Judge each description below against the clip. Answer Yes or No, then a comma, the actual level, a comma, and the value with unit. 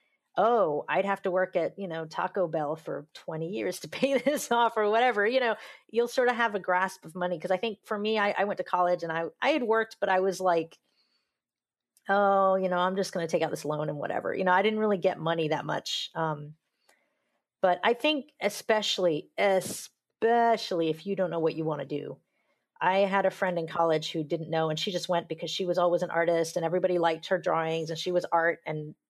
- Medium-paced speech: No, fast, 235 wpm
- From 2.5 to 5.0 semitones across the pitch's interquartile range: Yes, average, 3.6 semitones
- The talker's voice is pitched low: No, medium, 185 Hz